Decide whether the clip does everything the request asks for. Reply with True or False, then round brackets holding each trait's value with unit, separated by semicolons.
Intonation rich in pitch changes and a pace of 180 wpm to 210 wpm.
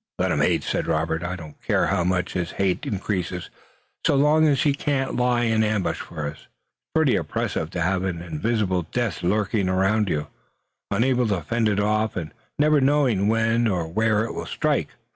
False (4.9 semitones; 190 wpm)